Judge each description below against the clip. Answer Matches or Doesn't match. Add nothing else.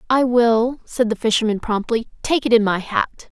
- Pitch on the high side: Matches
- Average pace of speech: Matches